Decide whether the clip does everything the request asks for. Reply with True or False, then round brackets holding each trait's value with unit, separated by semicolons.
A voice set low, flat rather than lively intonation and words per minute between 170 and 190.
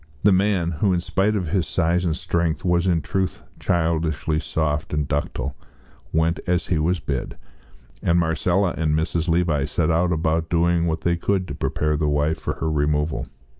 True (80 Hz; 2.1 semitones; 175 wpm)